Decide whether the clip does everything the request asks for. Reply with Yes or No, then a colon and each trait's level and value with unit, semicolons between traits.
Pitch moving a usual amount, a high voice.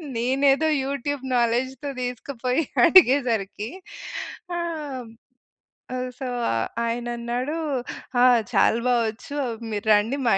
Yes: average, 3.0 semitones; very high, 250 Hz